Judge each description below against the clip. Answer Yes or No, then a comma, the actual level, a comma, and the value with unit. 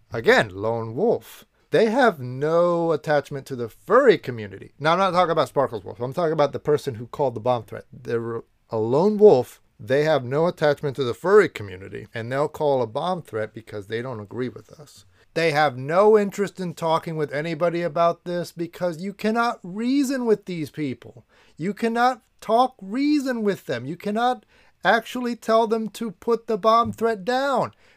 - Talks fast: No, average, 185 wpm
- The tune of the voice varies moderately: No, wide, 8.9 semitones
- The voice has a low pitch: No, medium, 165 Hz